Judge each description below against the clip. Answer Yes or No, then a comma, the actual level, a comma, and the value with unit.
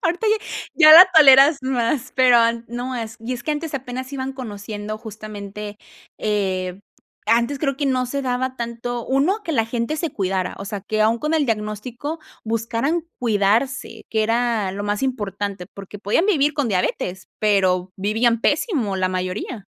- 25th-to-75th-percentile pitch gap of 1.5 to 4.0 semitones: No, average, 4.5 semitones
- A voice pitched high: Yes, high, 230 Hz